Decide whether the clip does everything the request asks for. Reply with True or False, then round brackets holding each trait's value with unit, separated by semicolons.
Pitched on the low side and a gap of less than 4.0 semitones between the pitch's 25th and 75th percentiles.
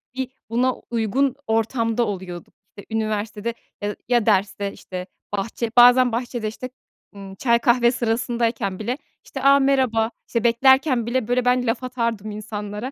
False (230 Hz; 2.8 semitones)